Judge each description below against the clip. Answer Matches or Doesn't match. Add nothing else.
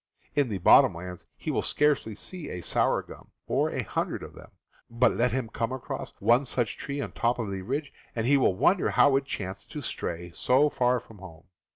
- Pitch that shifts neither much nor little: Doesn't match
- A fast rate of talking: Matches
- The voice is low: Matches